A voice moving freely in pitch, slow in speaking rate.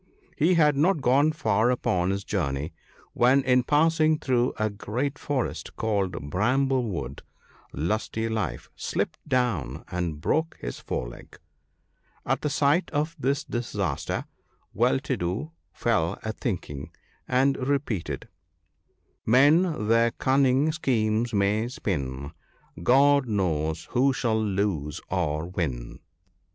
Yes: wide, 7.4 semitones; slow, 125 wpm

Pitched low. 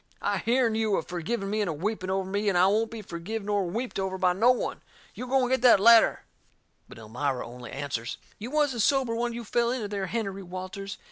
No: high, 205 Hz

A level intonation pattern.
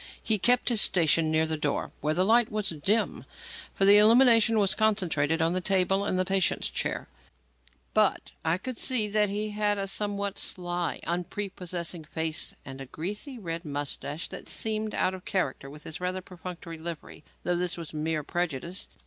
No: average, 4.2 semitones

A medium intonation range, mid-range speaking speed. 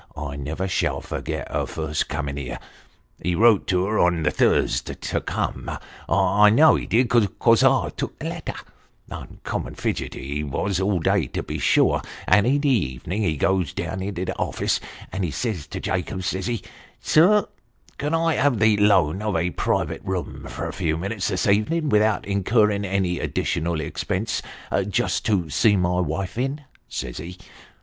Yes: average, 4.5 semitones; average, 180 wpm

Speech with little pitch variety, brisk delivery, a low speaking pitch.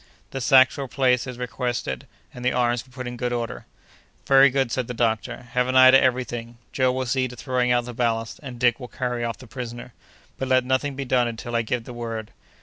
Yes: narrow, 1.4 semitones; fast, 240 wpm; low, 125 Hz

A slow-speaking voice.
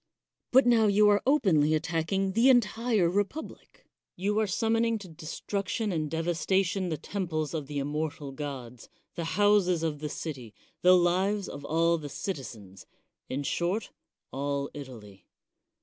No: average, 150 wpm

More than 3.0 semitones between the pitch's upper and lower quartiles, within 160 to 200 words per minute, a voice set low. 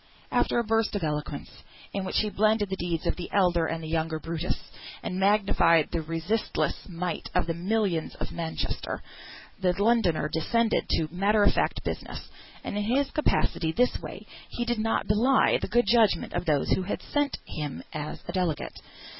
No: average, 4.9 semitones; average, 180 wpm; medium, 185 Hz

